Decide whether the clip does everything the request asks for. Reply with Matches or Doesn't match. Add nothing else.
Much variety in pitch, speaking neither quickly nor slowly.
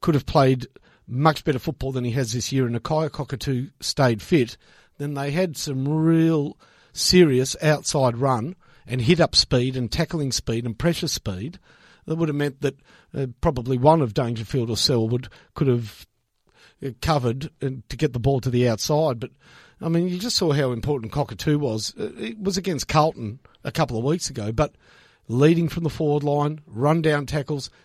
Doesn't match